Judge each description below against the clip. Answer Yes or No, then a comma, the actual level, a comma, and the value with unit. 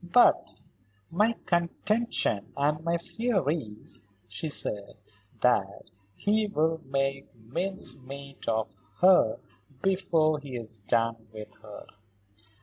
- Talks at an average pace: No, slow, 105 wpm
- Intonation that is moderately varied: No, wide, 7.5 semitones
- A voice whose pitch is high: No, medium, 140 Hz